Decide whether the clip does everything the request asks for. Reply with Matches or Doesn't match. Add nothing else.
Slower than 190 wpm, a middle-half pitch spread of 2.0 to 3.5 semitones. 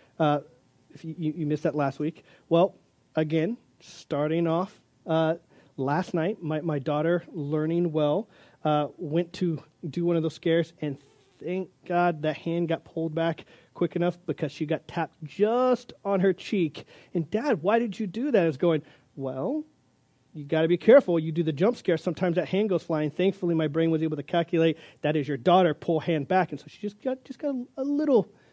Doesn't match